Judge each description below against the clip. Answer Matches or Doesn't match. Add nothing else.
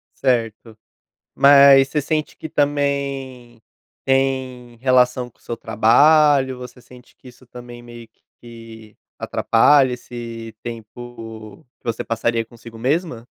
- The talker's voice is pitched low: Matches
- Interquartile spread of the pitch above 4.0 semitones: Doesn't match